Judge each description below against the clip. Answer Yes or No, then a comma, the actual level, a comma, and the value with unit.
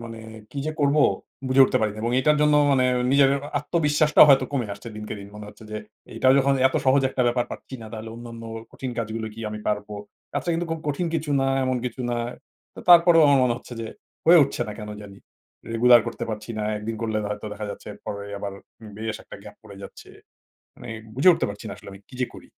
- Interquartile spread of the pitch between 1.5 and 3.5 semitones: No, average, 4.5 semitones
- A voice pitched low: Yes, low, 120 Hz